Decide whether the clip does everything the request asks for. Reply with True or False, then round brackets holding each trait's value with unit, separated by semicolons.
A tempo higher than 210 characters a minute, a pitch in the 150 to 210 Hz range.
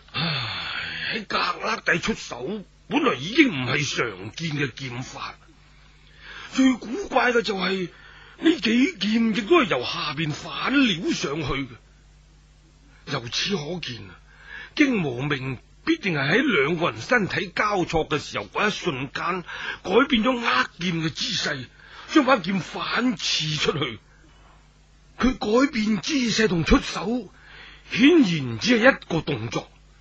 False (190 characters per minute; 190 Hz)